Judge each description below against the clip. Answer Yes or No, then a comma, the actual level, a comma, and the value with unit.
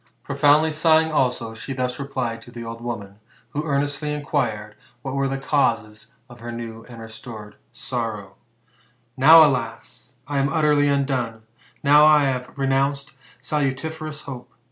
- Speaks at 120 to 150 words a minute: Yes, average, 145 wpm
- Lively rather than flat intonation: No, average, 3.8 semitones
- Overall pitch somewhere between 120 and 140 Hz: Yes, low, 135 Hz